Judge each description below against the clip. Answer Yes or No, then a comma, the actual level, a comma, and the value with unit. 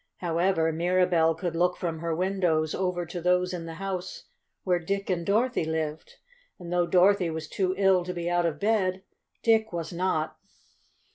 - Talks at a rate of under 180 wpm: Yes, average, 170 wpm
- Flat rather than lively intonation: Yes, narrow, 2.2 semitones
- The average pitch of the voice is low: No, medium, 180 Hz